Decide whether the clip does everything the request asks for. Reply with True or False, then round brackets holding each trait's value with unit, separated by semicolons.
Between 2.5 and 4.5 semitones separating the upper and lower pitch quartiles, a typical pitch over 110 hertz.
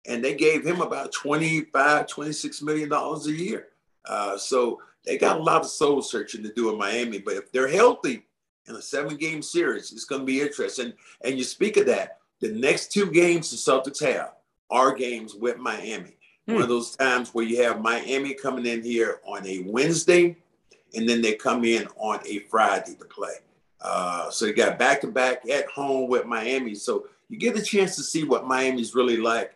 False (5.2 semitones; 135 Hz)